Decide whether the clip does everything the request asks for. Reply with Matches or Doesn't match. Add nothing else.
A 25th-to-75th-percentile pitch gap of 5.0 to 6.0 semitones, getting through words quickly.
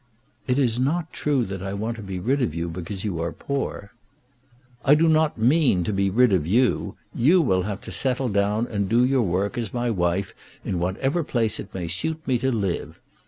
Matches